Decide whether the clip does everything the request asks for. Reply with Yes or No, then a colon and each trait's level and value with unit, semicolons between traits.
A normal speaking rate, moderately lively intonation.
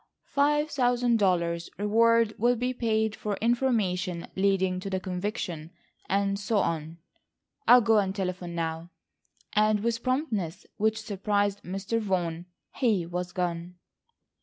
No: slow, 130 wpm; average, 4.1 semitones